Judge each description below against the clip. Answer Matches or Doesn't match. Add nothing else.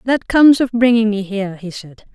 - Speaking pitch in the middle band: Doesn't match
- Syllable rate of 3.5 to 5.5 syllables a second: Doesn't match